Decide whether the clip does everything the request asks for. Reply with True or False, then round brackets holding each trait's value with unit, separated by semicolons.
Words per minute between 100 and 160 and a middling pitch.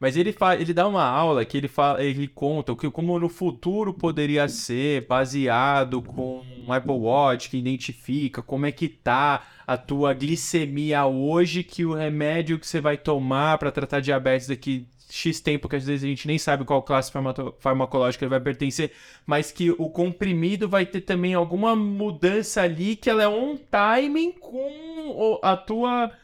False (180 wpm; 150 Hz)